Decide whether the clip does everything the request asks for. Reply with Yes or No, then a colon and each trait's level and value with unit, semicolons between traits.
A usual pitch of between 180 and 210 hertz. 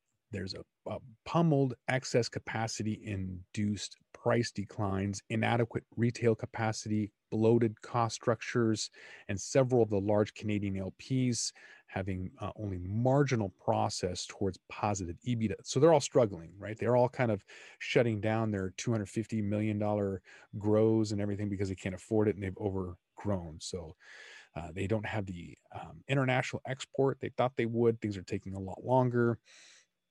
No: low, 110 Hz